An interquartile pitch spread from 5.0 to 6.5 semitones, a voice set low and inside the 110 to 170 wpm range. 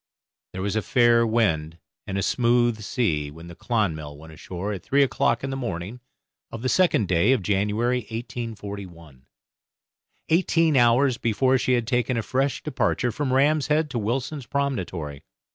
Yes: wide, 5.4 semitones; low, 115 Hz; average, 160 wpm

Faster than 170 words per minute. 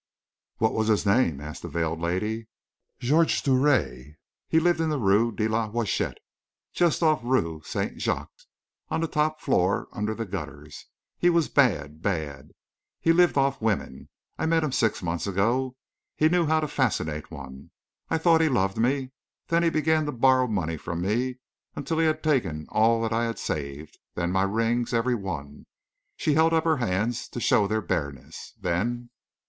Yes: average, 180 wpm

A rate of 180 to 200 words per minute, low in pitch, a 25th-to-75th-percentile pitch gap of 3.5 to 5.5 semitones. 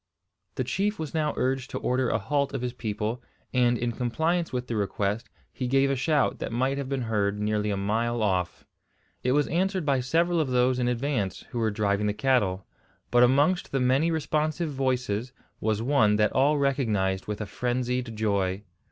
Yes: average, 190 wpm; low, 125 Hz; average, 4.5 semitones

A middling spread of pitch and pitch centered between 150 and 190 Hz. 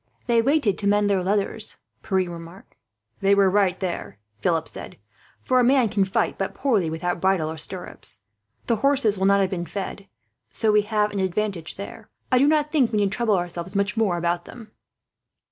No: average, 3.5 semitones; high, 200 Hz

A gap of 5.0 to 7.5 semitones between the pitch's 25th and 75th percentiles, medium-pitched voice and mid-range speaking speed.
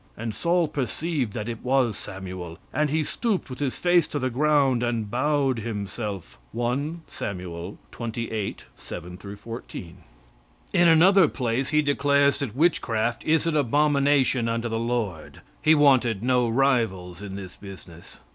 No: wide, 5.6 semitones; low, 120 Hz; average, 145 wpm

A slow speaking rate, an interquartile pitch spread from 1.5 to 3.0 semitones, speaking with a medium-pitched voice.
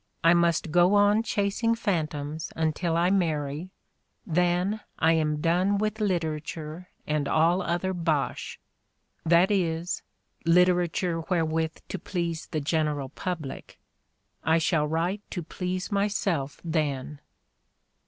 Yes: slow, 120 wpm; average, 2.7 semitones; medium, 170 Hz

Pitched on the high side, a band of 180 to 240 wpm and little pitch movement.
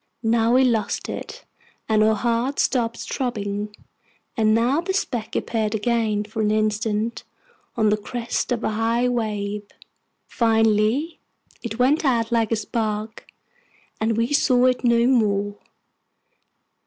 No: high, 225 Hz; slow, 135 wpm; narrow, 2.1 semitones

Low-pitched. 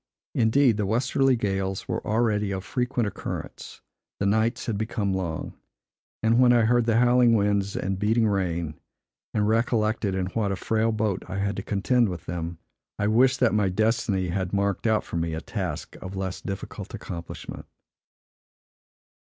Yes: low, 105 Hz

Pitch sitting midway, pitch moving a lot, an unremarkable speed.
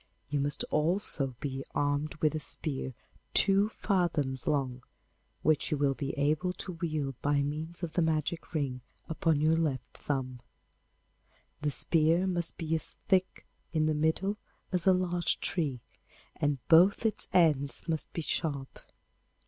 No: medium, 155 Hz; average, 3.2 semitones; average, 150 wpm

